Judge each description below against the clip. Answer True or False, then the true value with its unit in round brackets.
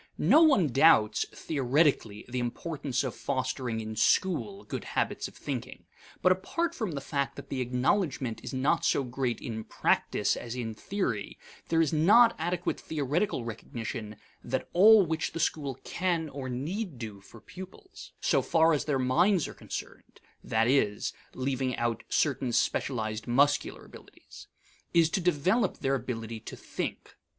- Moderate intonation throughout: False (6.1 semitones)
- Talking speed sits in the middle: True (155 wpm)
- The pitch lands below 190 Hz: True (140 Hz)